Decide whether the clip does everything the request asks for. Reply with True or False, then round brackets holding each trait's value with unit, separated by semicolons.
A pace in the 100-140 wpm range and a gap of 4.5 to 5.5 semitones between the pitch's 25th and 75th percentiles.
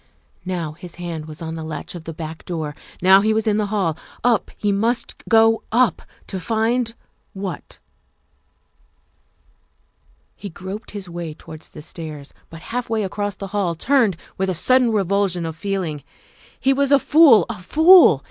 False (170 wpm; 5.2 semitones)